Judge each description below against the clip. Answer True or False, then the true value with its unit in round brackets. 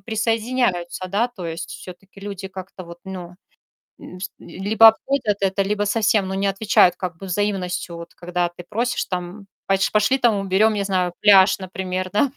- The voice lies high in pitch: True (195 Hz)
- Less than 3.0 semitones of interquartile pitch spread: True (2.6 semitones)